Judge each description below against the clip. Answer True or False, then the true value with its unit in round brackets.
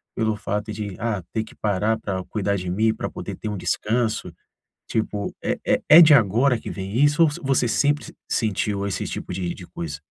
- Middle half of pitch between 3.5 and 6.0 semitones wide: False (3.1 semitones)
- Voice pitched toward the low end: True (105 Hz)